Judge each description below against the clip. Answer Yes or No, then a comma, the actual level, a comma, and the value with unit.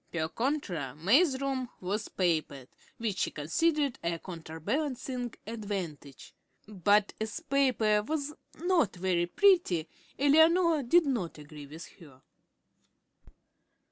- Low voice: No, high, 215 Hz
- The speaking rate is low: Yes, slow, 110 wpm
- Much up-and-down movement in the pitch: Yes, wide, 8.9 semitones